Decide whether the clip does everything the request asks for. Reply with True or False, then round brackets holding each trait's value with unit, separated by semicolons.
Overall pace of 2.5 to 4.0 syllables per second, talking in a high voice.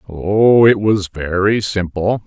False (3.4 syllables/s; 100 Hz)